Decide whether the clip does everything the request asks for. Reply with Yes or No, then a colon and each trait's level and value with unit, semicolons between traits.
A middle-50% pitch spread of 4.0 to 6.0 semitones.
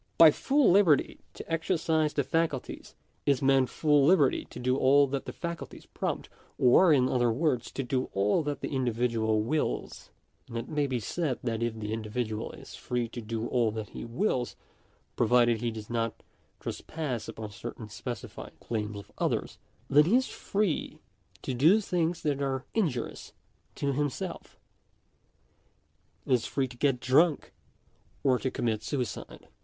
Yes: average, 4.5 semitones